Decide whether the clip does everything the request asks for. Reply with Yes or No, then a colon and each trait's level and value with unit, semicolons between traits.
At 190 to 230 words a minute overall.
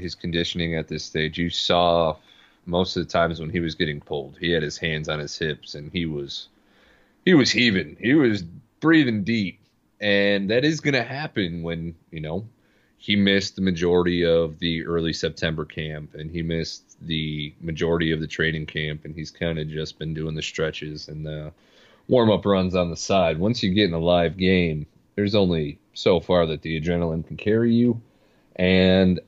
Yes: average, 195 wpm